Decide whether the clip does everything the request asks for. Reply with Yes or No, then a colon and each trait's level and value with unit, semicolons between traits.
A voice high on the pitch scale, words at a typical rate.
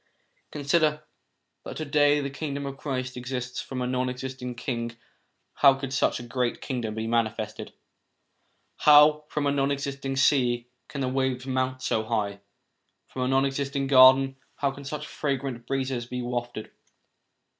No: low, 130 Hz; average, 155 wpm